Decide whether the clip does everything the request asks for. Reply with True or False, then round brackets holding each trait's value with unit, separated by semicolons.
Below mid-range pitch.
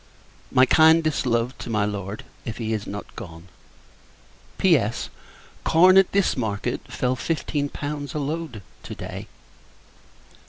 True (130 Hz)